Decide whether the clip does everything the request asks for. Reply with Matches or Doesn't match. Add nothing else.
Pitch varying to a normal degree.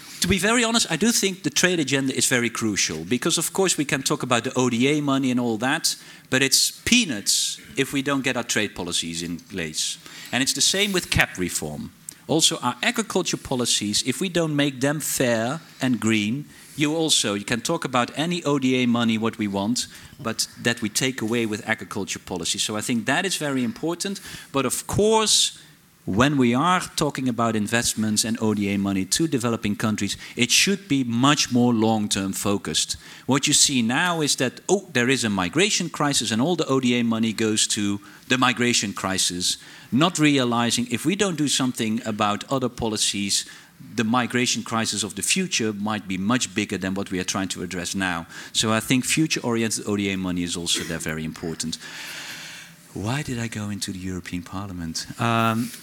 Doesn't match